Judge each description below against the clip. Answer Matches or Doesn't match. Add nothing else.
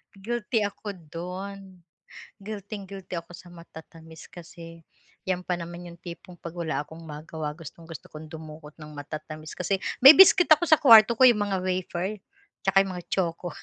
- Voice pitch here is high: Doesn't match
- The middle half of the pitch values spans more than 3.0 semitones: Matches